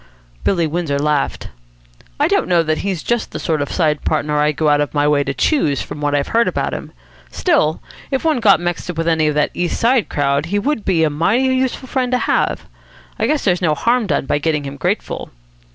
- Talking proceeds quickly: Yes, fast, 230 wpm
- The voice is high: No, medium, 165 Hz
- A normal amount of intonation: No, wide, 6.9 semitones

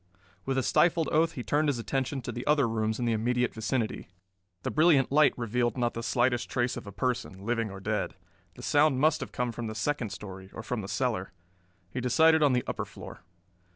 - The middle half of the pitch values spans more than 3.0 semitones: Yes, average, 3.5 semitones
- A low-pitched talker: Yes, low, 125 Hz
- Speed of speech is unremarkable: No, fast, 215 wpm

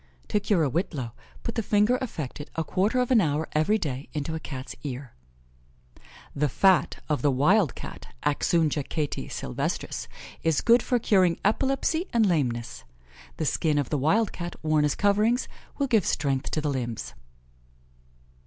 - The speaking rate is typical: Yes, average, 160 wpm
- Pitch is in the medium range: Yes, medium, 160 Hz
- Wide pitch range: Yes, wide, 6.6 semitones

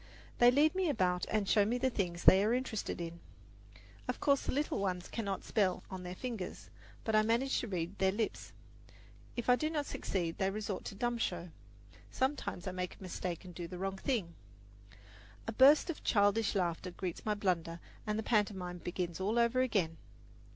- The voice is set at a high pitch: Yes, high, 200 Hz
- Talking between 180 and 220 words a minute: Yes, average, 190 wpm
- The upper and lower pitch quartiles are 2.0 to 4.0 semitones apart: No, average, 4.8 semitones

